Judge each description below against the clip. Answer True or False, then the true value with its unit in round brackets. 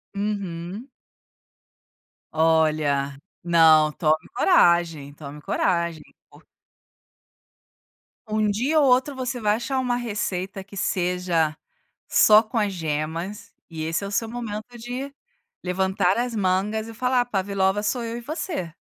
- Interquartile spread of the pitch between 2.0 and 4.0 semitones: False (5.6 semitones)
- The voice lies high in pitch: True (195 Hz)